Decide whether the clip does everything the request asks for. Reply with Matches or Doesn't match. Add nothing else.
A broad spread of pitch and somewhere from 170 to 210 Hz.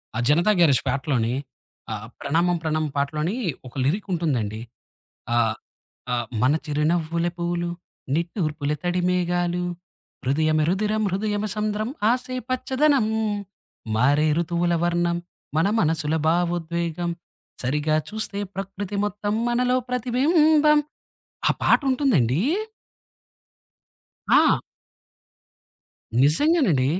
Matches